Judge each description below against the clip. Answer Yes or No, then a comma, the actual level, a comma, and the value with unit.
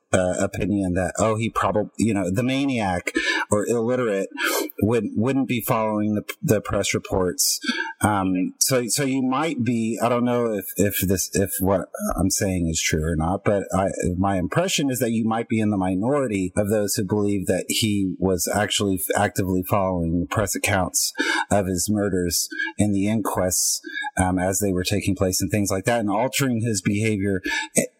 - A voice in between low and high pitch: No, low, 100 Hz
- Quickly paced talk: No, average, 180 wpm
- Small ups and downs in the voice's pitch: No, average, 3.1 semitones